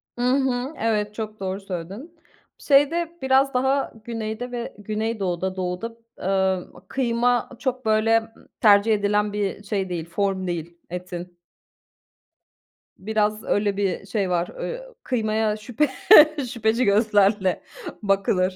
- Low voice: No, high, 215 Hz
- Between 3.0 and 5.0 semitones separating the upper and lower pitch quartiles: Yes, average, 3.7 semitones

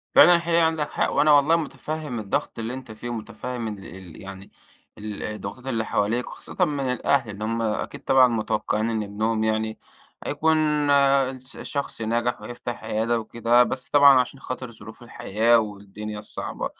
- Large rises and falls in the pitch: No, average, 3.8 semitones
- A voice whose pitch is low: Yes, low, 115 Hz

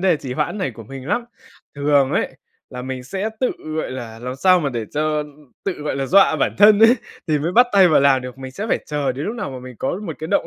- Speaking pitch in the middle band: Yes, medium, 145 Hz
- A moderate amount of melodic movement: No, wide, 6.5 semitones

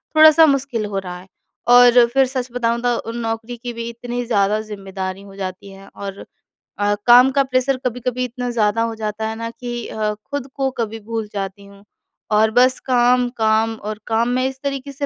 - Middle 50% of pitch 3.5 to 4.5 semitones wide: No, average, 2.9 semitones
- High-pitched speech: Yes, high, 230 Hz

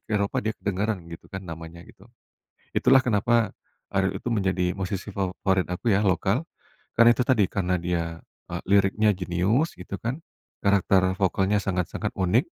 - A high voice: No, low, 100 Hz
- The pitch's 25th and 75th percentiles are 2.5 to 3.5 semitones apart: Yes, average, 2.9 semitones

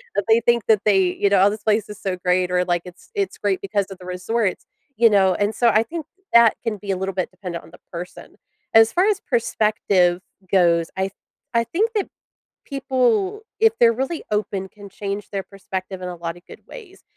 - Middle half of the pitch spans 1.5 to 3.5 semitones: No, average, 4.0 semitones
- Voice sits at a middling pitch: No, high, 205 Hz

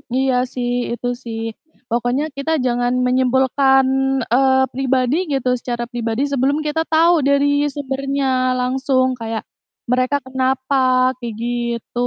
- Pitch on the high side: Yes, very high, 260 Hz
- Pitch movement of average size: No, narrow, 1.8 semitones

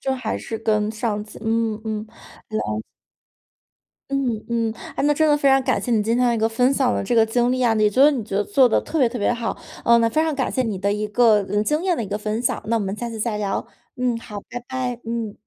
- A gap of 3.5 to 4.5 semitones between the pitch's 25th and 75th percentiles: No, average, 2.8 semitones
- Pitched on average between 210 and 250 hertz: Yes, high, 230 Hz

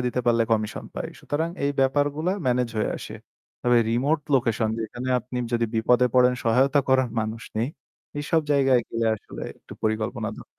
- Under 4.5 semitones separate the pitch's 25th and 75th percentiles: Yes, average, 2.7 semitones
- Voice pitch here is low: Yes, low, 125 Hz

